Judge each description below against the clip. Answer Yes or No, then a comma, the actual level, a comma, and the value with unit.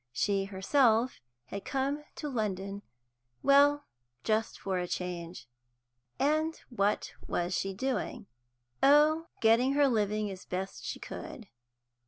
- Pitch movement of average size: No, wide, 6.2 semitones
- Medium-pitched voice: No, high, 220 Hz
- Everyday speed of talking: No, slow, 120 wpm